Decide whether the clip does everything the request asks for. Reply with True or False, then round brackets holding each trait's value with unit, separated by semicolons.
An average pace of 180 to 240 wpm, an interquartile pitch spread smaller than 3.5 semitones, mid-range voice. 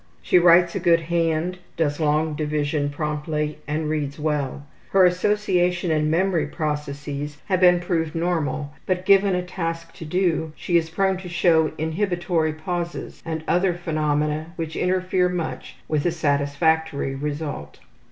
False (145 wpm; 2.8 semitones; 160 Hz)